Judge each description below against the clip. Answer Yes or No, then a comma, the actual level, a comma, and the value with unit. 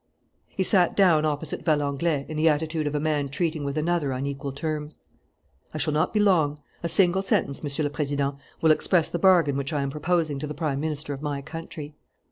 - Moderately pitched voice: Yes, medium, 150 Hz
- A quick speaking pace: Yes, fast, 210 wpm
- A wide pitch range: No, narrow, 2.4 semitones